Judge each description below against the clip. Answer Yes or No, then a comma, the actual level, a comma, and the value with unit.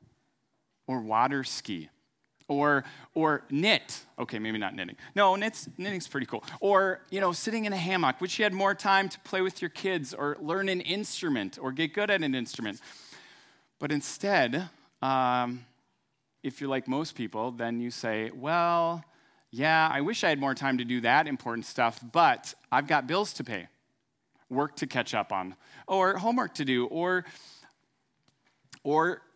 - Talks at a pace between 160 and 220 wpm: Yes, average, 170 wpm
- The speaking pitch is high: No, medium, 155 Hz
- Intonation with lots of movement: Yes, wide, 6.7 semitones